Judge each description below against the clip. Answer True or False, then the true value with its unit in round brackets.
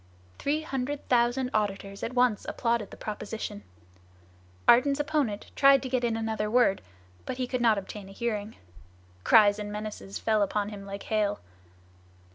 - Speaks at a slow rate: False (155 wpm)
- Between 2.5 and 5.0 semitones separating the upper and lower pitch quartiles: True (3.4 semitones)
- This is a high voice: True (220 Hz)